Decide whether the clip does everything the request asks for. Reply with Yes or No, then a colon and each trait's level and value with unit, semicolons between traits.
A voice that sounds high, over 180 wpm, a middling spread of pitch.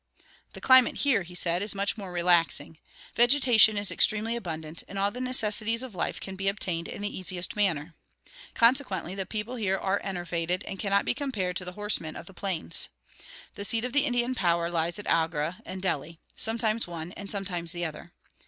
Yes: high, 195 Hz; average, 190 wpm; average, 4.3 semitones